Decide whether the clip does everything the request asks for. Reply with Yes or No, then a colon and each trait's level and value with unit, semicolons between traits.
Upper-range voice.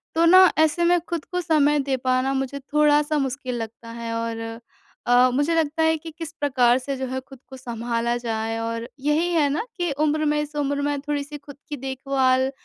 Yes: very high, 280 Hz